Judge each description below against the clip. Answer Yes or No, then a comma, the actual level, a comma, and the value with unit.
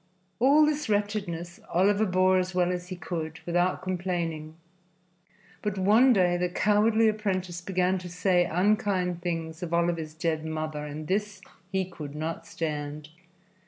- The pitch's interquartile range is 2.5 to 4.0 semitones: Yes, average, 3.0 semitones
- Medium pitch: Yes, medium, 180 Hz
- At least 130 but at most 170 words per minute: Yes, average, 145 wpm